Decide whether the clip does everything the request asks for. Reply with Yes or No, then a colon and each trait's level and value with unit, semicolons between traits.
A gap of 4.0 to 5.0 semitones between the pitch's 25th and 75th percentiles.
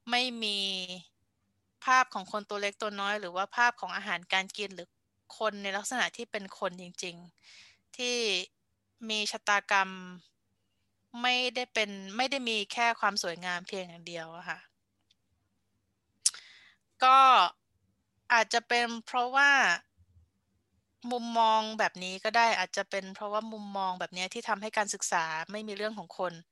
Yes: average, 4.7 semitones